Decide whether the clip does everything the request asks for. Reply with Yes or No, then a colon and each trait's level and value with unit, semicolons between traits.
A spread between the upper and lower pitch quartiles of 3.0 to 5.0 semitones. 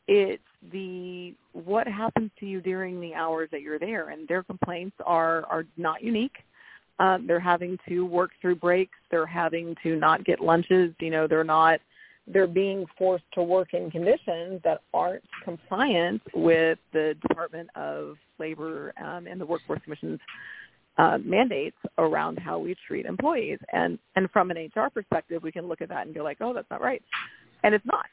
No: narrow, 2.6 semitones